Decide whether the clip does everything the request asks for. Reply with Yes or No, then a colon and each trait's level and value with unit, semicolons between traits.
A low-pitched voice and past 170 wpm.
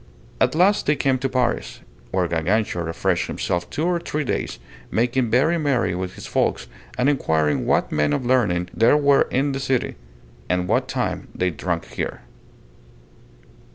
No: low, 120 Hz; average, 165 wpm